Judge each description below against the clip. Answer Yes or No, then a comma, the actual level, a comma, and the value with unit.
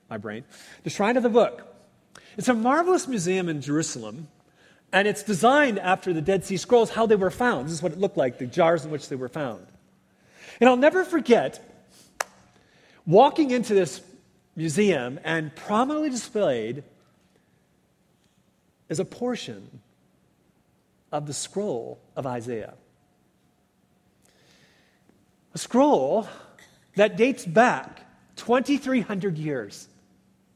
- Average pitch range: No, wide, 7.2 semitones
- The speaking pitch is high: Yes, high, 200 Hz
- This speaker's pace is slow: Yes, slow, 125 wpm